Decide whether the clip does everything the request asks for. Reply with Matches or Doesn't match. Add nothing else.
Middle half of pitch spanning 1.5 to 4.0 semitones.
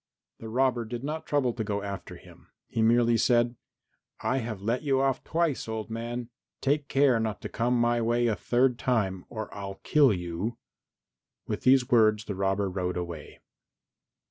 Matches